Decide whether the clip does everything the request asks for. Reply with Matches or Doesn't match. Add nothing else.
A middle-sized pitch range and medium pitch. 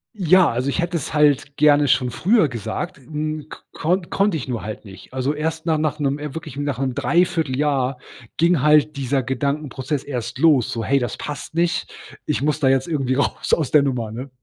Matches